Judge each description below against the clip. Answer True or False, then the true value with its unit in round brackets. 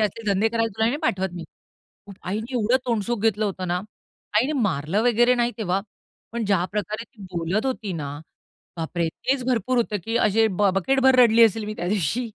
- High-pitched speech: True (215 Hz)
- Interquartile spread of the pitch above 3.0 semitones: True (3.7 semitones)